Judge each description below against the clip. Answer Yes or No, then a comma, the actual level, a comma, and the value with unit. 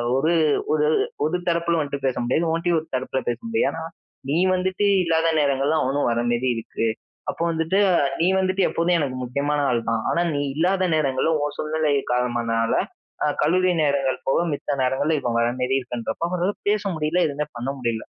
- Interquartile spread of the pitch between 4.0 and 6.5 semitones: Yes, average, 4.5 semitones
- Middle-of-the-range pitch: Yes, medium, 145 Hz